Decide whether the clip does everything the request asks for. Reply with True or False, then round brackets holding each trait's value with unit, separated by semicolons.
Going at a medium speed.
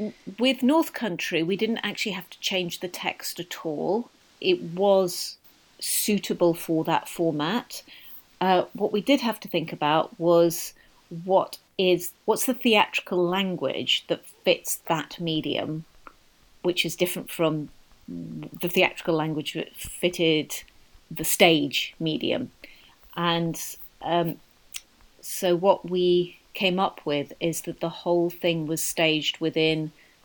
False (130 wpm)